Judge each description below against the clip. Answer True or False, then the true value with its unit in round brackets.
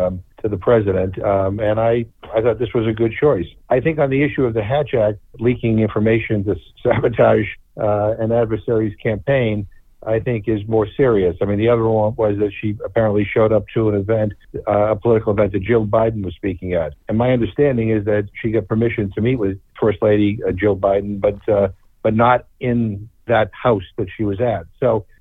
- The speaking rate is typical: False (210 wpm)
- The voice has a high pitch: False (110 Hz)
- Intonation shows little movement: True (2.1 semitones)